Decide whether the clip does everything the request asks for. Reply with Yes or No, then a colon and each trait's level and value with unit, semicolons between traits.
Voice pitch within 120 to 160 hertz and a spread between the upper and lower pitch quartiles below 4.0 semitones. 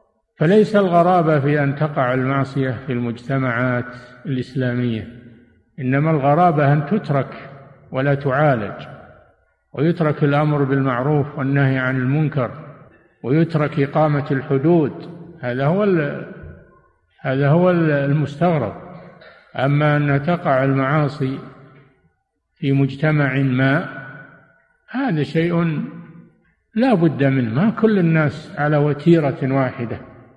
Yes: medium, 140 Hz; average, 2.8 semitones